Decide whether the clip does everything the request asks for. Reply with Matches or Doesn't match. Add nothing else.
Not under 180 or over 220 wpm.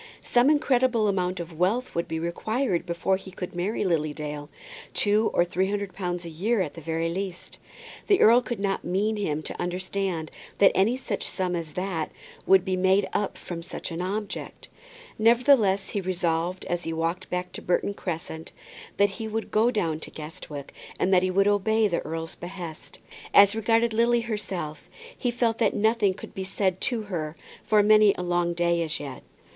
Matches